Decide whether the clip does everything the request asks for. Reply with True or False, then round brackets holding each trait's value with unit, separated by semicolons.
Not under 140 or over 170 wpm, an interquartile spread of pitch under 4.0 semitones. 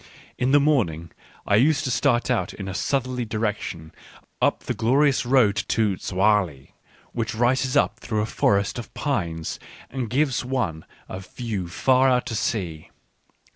False (155 wpm; 4.9 semitones)